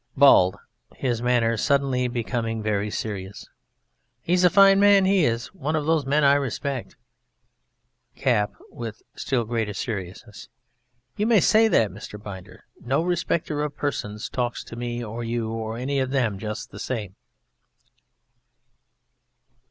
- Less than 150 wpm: Yes, average, 140 wpm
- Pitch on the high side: No, low, 120 Hz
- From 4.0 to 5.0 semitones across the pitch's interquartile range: Yes, average, 4.7 semitones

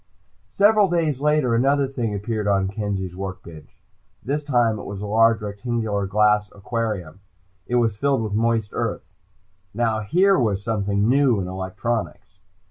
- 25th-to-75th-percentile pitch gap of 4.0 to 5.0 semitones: No, average, 3.5 semitones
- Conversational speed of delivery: Yes, average, 150 wpm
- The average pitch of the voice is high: No, low, 110 Hz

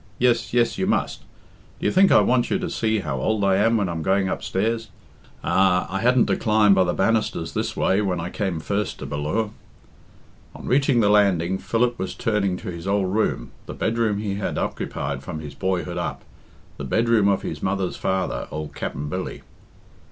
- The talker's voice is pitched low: Yes, low, 100 Hz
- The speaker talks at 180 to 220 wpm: Yes, average, 195 wpm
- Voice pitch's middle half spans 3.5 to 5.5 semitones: Yes, average, 3.9 semitones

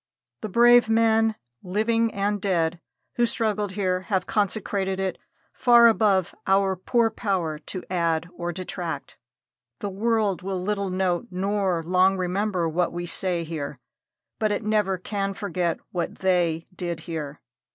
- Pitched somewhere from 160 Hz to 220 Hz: Yes, high, 190 Hz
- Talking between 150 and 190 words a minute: No, average, 140 wpm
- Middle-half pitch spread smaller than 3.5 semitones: Yes, average, 3.1 semitones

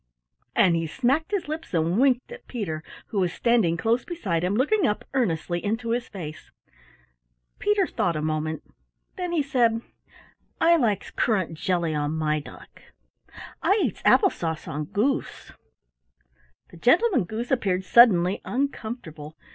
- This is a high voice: Yes, high, 215 Hz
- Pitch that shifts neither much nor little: No, wide, 8.2 semitones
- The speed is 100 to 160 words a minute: Yes, average, 145 wpm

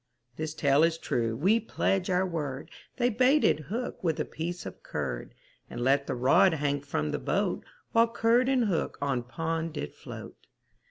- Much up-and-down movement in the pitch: Yes, wide, 7.0 semitones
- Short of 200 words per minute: Yes, average, 175 wpm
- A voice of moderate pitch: Yes, medium, 160 Hz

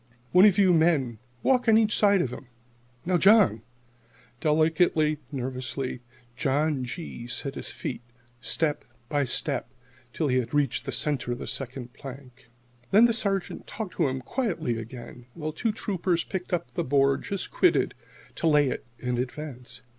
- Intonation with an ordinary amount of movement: No, wide, 5.8 semitones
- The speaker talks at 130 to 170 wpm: Yes, average, 160 wpm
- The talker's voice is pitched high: No, medium, 145 Hz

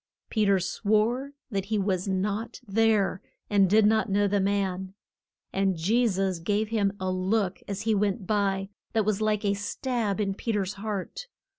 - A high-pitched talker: Yes, high, 200 Hz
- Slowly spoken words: No, average, 175 wpm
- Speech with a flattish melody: Yes, narrow, 2.0 semitones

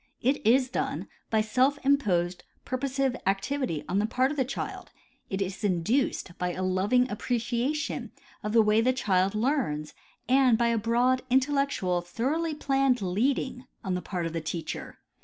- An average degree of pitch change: No, wide, 5.7 semitones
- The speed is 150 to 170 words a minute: Yes, average, 160 wpm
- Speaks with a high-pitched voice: Yes, high, 235 Hz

